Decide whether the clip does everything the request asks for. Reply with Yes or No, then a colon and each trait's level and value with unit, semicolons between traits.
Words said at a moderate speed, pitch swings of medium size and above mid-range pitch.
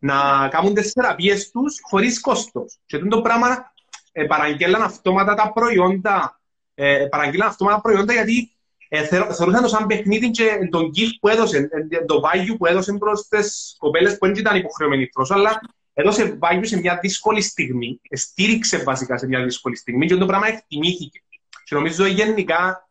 No: fast, 175 wpm; average, 4.9 semitones; high, 195 Hz